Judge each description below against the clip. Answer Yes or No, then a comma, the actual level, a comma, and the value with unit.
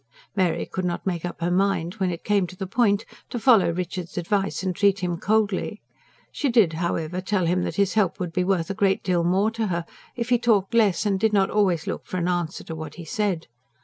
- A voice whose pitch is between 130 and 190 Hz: Yes, medium, 185 Hz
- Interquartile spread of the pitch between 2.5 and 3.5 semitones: Yes, average, 2.9 semitones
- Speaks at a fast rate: Yes, fast, 235 wpm